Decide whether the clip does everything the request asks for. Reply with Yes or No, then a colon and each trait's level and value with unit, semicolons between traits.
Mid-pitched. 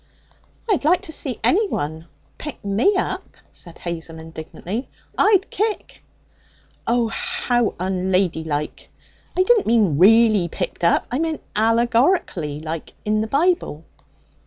No: high, 220 Hz